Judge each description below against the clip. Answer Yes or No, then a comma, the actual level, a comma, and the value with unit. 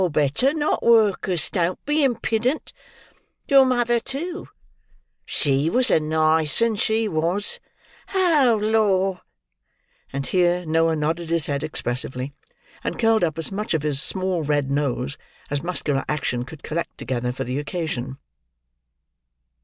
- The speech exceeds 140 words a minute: No, slow, 135 wpm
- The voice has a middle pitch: Yes, medium, 170 Hz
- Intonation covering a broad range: Yes, wide, 7.2 semitones